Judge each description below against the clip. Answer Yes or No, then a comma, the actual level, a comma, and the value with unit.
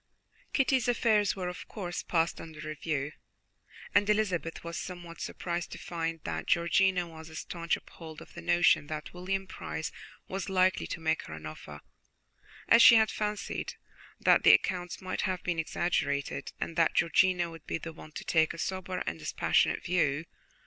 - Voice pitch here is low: No, medium, 175 Hz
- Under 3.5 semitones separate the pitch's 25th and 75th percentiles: Yes, average, 2.7 semitones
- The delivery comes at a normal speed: Yes, average, 170 wpm